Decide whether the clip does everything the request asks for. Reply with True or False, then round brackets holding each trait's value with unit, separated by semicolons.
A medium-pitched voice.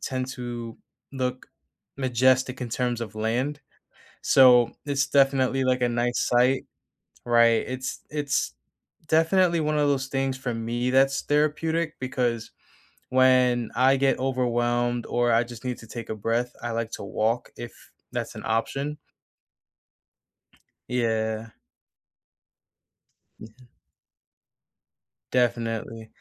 False (125 Hz)